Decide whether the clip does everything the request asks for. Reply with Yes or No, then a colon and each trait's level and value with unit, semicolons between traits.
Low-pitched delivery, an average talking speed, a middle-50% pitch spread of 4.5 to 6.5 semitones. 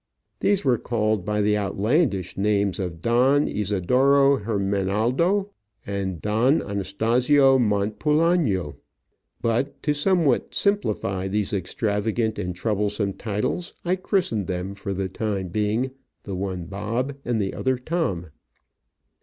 No: low, 105 Hz; slow, 120 wpm; average, 5.1 semitones